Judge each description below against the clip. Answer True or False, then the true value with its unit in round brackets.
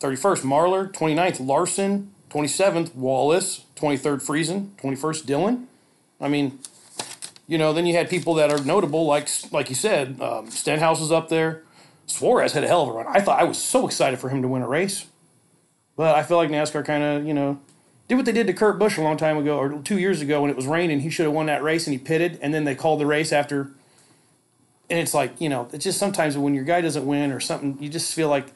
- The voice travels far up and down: False (2.9 semitones)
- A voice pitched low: False (155 Hz)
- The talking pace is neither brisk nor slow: False (235 wpm)